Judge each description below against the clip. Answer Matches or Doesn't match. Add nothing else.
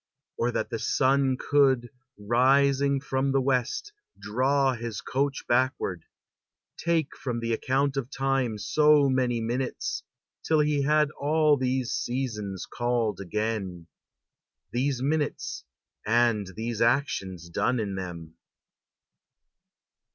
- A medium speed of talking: Doesn't match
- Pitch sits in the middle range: Doesn't match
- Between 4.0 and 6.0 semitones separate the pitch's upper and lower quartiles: Doesn't match